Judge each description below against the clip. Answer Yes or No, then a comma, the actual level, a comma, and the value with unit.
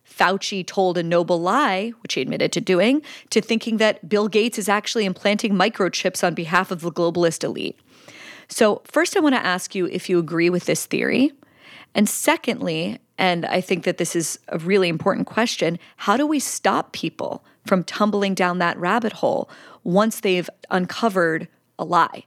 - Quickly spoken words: No, average, 180 wpm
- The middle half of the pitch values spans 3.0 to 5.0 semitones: Yes, average, 4.0 semitones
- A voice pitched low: No, high, 195 Hz